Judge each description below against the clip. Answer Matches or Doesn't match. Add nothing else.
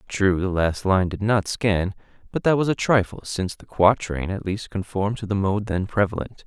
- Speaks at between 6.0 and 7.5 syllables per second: Doesn't match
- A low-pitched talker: Matches